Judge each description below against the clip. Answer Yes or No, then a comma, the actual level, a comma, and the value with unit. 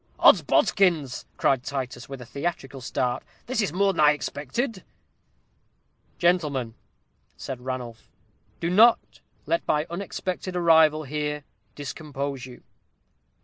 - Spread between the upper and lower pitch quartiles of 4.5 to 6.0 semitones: Yes, average, 5.0 semitones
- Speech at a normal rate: No, slow, 115 wpm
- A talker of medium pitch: Yes, medium, 150 Hz